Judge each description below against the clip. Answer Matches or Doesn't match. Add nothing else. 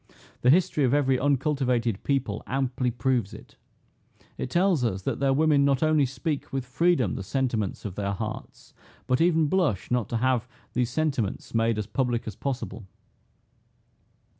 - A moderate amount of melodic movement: Matches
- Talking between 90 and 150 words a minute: Doesn't match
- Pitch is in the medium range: Doesn't match